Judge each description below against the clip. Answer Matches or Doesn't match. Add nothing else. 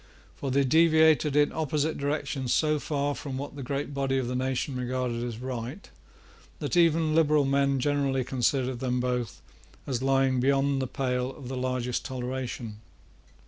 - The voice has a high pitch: Doesn't match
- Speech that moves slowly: Doesn't match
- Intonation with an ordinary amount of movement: Doesn't match